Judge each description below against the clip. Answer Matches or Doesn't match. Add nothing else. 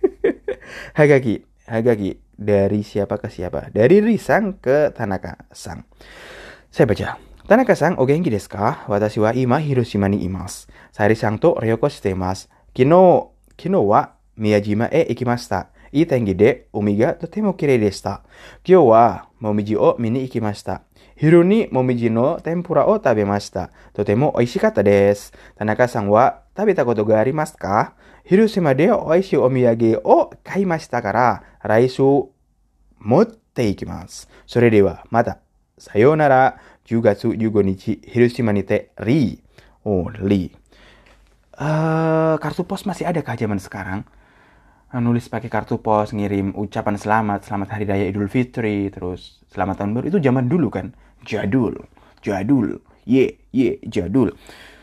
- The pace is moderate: Doesn't match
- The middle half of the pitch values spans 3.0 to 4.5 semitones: Doesn't match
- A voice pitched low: Matches